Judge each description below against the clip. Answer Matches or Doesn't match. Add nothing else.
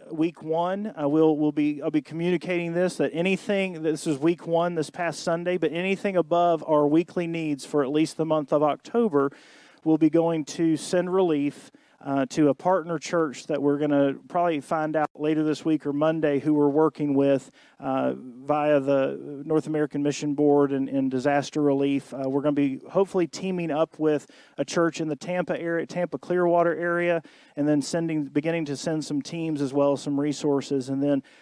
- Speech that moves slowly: Doesn't match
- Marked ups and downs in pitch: Doesn't match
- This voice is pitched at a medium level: Matches